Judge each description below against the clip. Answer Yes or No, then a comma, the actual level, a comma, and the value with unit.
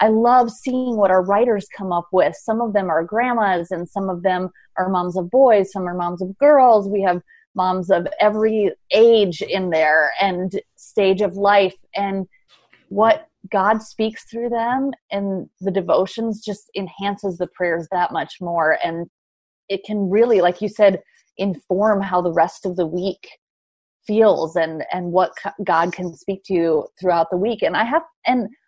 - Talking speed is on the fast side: No, average, 180 wpm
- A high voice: Yes, high, 195 Hz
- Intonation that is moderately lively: Yes, average, 3.3 semitones